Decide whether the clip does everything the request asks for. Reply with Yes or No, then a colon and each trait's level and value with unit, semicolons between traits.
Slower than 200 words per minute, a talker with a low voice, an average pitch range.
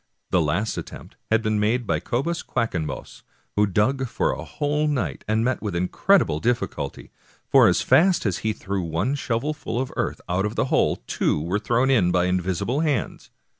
No: average, 180 wpm; low, 110 Hz; wide, 6.2 semitones